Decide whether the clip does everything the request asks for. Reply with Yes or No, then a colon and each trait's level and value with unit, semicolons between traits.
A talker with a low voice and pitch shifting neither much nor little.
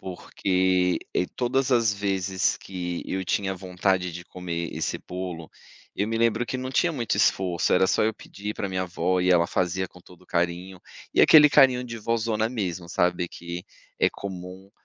Yes: very low, 95 Hz; average, 3.5 semitones